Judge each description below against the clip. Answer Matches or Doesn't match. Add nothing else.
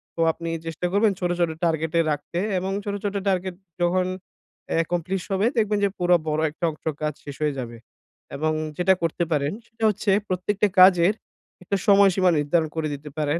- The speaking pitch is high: Doesn't match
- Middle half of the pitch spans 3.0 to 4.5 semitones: Matches